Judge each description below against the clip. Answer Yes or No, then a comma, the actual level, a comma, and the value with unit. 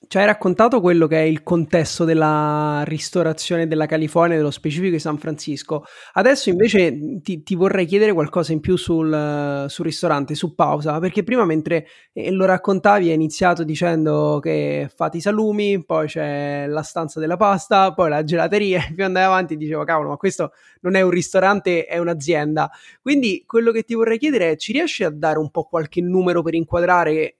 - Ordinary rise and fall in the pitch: Yes, average, 3.4 semitones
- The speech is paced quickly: Yes, fast, 180 wpm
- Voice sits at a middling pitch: Yes, medium, 170 Hz